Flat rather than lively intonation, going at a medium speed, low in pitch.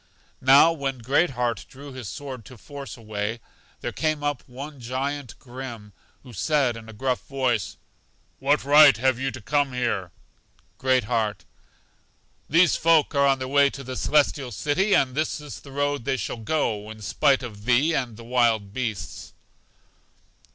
No: average, 3.5 semitones; average, 170 wpm; low, 130 Hz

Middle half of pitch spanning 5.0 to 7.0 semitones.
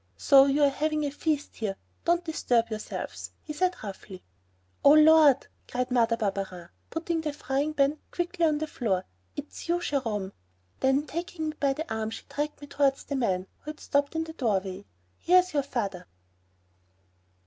Yes: wide, 5.4 semitones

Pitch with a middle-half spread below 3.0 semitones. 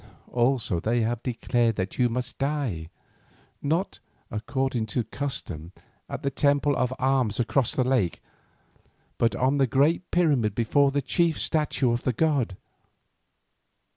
No: average, 3.7 semitones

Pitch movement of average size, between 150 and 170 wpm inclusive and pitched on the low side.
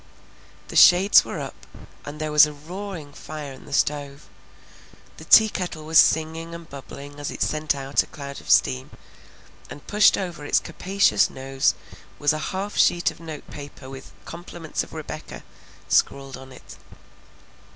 No: average, 3.3 semitones; average, 160 wpm; medium, 150 Hz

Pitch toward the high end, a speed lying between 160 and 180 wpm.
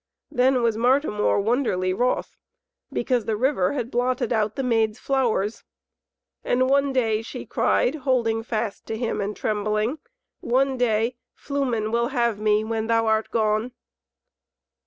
No: high, 230 Hz; average, 140 wpm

